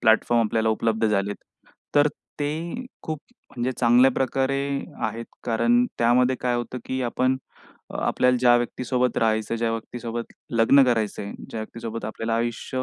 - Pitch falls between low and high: No, low, 120 Hz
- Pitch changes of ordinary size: No, narrow, 2.0 semitones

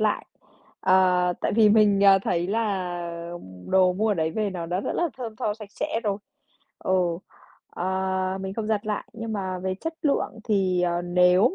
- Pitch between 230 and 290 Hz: No, high, 195 Hz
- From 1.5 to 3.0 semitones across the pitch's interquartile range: Yes, average, 2.7 semitones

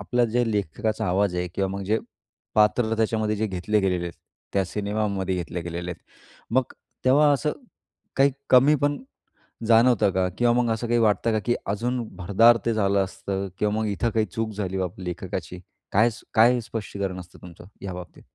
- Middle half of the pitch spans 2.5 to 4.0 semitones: Yes, average, 3.7 semitones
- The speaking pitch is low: Yes, low, 105 Hz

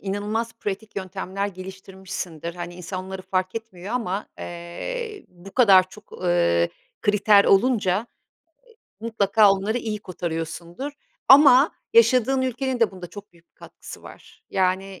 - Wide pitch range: No, average, 3.6 semitones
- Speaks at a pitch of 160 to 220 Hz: Yes, high, 195 Hz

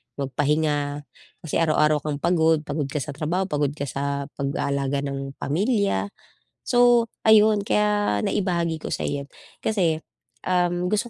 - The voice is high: No, medium, 155 Hz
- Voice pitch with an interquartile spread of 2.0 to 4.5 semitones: No, average, 5.0 semitones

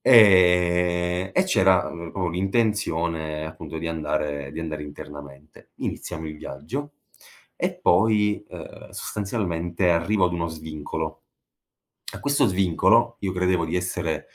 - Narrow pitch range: No, average, 3.4 semitones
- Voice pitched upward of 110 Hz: No, very low, 85 Hz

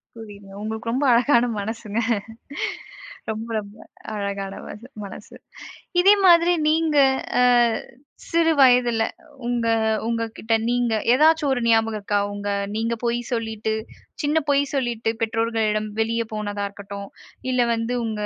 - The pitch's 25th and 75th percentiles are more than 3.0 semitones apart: No, narrow, 2.5 semitones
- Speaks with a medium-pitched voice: No, high, 230 Hz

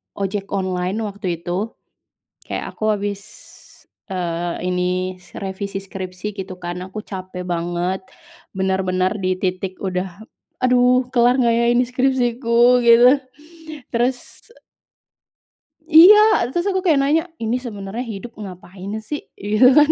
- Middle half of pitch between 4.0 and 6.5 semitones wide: Yes, average, 4.9 semitones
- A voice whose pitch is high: Yes, high, 200 Hz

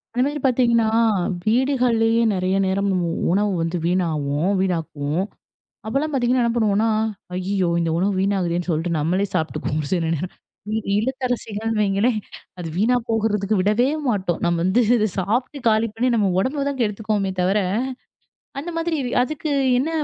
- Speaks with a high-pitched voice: Yes, high, 210 Hz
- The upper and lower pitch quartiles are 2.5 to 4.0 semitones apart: No, average, 4.7 semitones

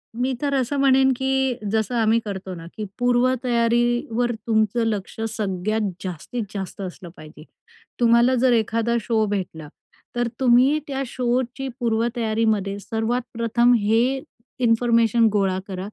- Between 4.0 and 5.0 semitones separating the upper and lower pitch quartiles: No, narrow, 2.6 semitones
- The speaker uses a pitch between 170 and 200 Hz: No, high, 230 Hz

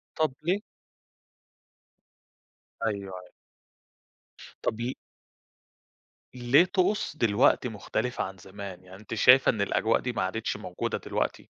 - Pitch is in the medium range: No, low, 110 Hz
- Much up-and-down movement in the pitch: No, average, 4.6 semitones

